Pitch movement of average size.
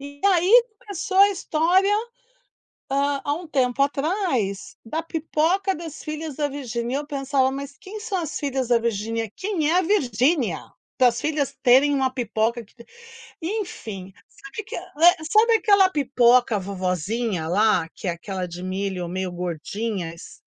No: wide, 7.2 semitones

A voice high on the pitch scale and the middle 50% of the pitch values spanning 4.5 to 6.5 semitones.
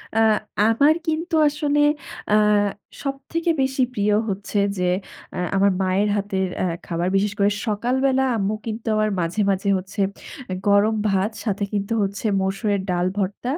Yes: high, 205 Hz; average, 4.8 semitones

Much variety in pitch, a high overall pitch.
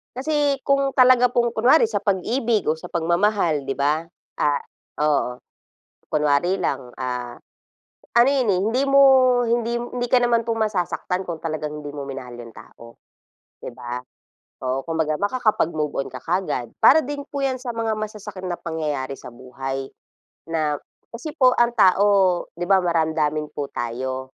No: wide, 8.7 semitones; medium, 175 Hz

